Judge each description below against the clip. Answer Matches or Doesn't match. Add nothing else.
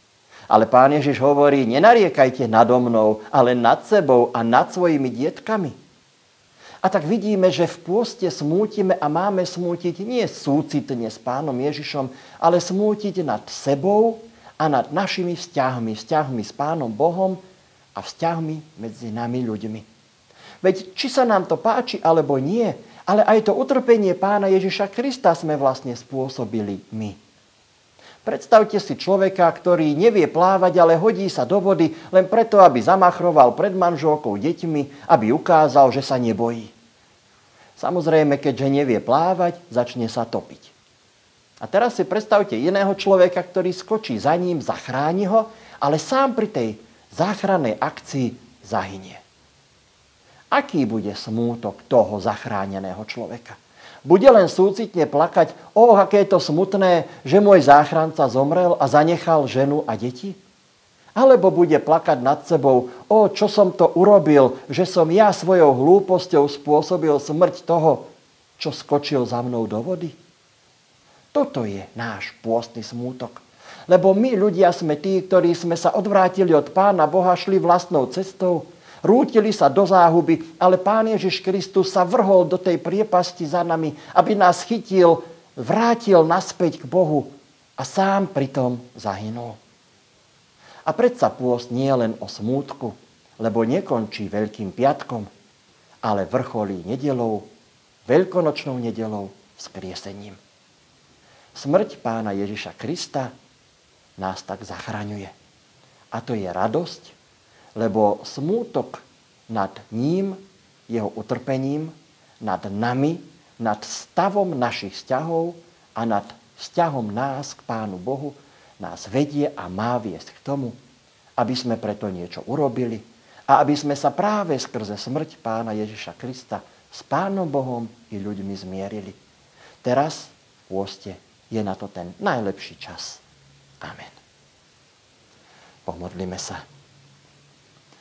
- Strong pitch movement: Matches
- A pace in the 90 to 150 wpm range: Matches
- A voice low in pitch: Doesn't match